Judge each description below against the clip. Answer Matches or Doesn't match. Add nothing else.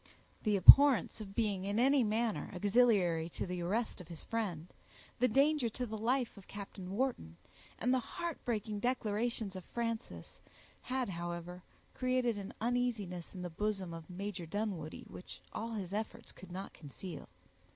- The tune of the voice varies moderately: Matches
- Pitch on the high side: Matches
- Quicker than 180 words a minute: Doesn't match